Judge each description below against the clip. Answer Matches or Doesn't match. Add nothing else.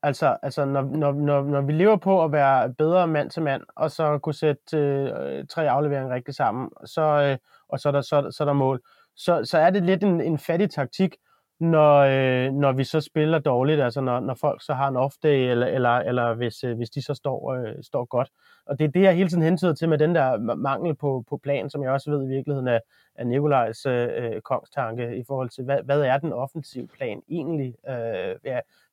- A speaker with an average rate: Doesn't match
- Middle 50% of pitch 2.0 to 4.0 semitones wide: Matches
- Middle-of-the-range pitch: Matches